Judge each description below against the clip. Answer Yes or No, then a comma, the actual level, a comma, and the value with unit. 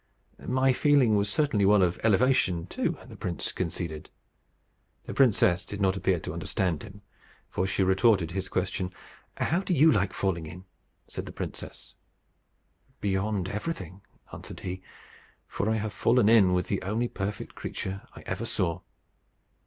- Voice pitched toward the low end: Yes, very low, 95 Hz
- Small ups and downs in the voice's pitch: No, average, 3.3 semitones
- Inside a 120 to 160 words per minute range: Yes, average, 155 wpm